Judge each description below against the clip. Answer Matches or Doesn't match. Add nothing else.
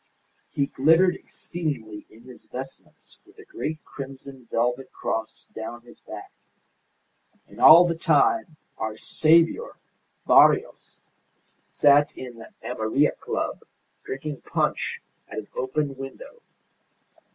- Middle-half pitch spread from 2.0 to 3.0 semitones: Doesn't match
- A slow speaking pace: Matches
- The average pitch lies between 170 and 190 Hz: Doesn't match